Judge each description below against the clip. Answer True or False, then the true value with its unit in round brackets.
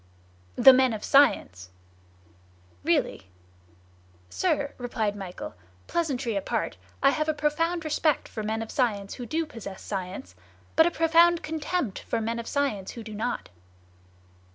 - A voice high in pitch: True (245 Hz)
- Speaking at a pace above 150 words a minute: False (145 wpm)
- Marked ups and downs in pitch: True (6.6 semitones)